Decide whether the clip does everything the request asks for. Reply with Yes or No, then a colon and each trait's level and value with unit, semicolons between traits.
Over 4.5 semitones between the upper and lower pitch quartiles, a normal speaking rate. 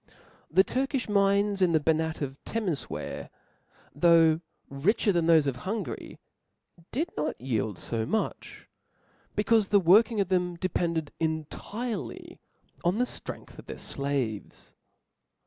No: average, 5.1 semitones; slow, 130 wpm